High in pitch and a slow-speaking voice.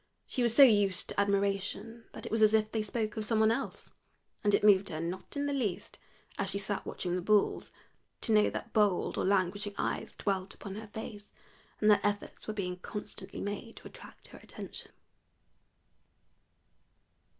No: high, 205 Hz; average, 185 wpm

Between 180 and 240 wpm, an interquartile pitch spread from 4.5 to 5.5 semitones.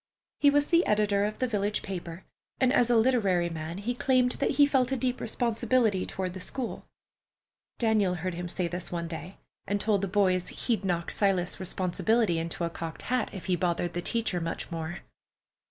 Yes: average, 190 wpm; average, 5.1 semitones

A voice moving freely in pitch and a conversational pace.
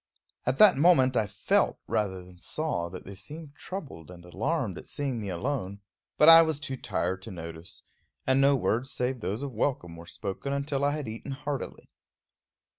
Yes: wide, 7.2 semitones; average, 185 wpm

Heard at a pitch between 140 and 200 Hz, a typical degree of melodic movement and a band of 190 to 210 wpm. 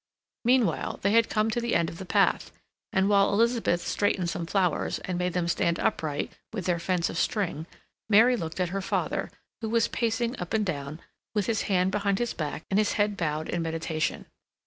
Yes: high, 190 Hz; average, 4.5 semitones; average, 200 wpm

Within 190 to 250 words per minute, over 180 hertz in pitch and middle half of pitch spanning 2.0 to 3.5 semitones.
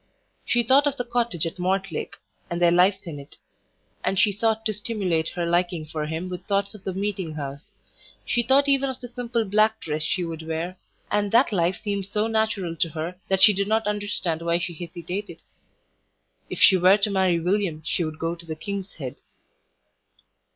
No: average, 195 wpm; high, 190 Hz; average, 4.1 semitones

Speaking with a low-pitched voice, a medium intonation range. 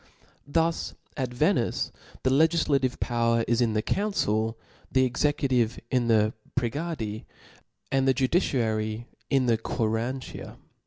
Yes: low, 125 Hz; average, 3.5 semitones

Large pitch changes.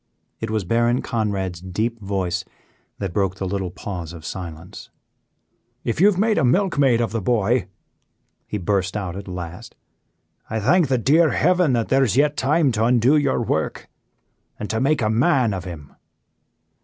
Yes: wide, 5.8 semitones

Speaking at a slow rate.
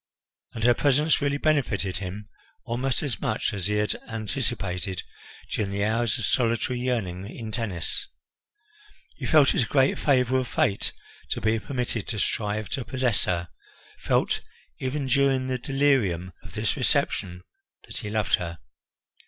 No: average, 155 wpm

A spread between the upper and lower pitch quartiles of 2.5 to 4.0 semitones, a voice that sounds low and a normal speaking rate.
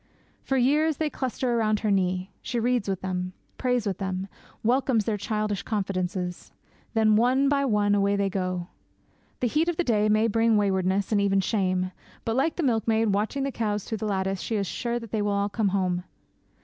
No: average, 3.5 semitones; high, 210 Hz; average, 195 wpm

